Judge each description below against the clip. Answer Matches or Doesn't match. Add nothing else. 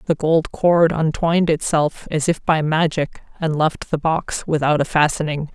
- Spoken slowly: Doesn't match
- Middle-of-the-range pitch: Matches